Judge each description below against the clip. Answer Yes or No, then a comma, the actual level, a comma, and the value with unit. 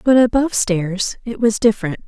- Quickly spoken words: No, average, 175 wpm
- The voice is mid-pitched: No, high, 220 Hz